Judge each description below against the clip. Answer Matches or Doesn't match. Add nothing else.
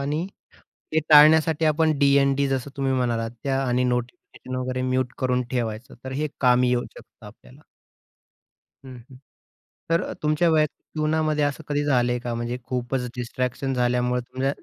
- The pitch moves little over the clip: Doesn't match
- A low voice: Matches